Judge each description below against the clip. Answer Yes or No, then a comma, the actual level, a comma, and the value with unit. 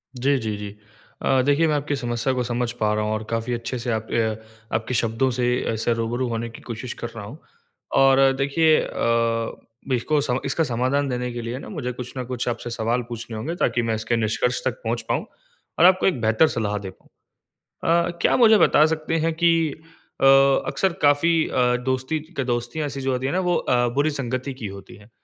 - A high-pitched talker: No, low, 125 Hz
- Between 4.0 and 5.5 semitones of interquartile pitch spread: No, average, 3.5 semitones